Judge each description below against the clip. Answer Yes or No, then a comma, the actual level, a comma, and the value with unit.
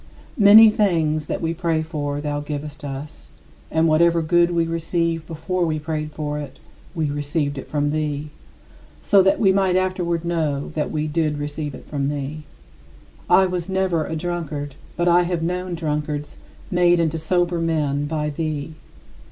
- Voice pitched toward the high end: No, medium, 160 Hz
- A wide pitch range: No, average, 2.7 semitones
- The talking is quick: No, average, 165 wpm